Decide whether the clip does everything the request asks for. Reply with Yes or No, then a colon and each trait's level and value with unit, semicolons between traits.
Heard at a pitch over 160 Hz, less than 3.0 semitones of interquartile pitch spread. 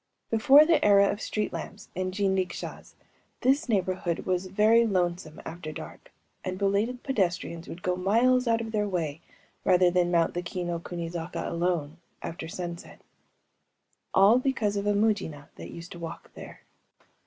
No: medium, 185 Hz; average, 3.5 semitones